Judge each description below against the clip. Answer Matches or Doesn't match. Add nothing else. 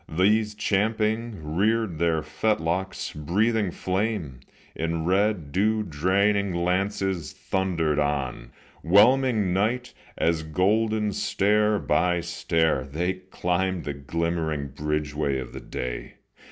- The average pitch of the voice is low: Matches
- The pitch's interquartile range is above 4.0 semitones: Matches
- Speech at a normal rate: Doesn't match